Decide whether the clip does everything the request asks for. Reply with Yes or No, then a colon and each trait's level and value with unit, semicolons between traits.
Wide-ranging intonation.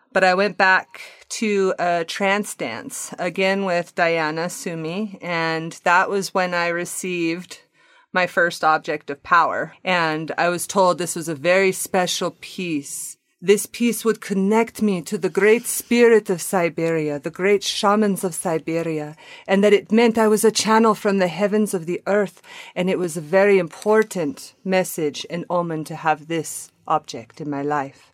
No: average, 3.7 semitones